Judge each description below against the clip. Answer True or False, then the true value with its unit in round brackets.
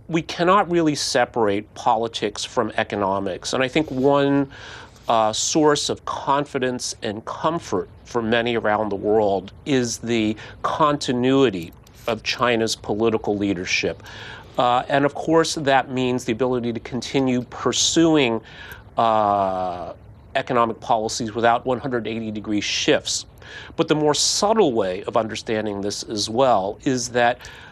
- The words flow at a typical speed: False (130 wpm)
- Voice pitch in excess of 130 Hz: False (120 Hz)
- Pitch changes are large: False (3.8 semitones)